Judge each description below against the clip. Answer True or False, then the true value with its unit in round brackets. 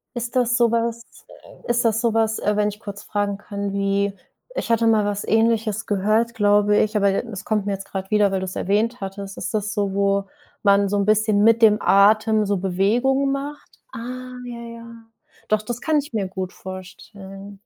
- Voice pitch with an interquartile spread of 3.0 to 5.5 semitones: False (2.5 semitones)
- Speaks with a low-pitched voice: False (210 Hz)